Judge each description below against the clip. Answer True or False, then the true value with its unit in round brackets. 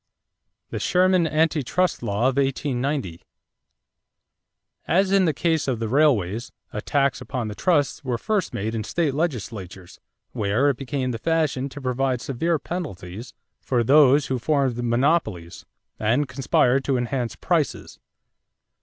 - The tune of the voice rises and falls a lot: False (4.5 semitones)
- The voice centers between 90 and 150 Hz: True (135 Hz)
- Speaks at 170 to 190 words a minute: False (135 wpm)